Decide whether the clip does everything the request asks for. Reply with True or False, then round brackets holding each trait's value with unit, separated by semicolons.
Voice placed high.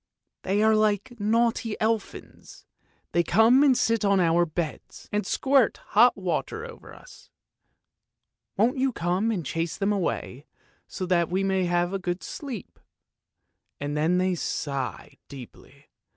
True (195 Hz)